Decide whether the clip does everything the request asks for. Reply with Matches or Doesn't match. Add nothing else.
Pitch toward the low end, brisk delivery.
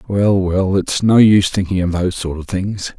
Matches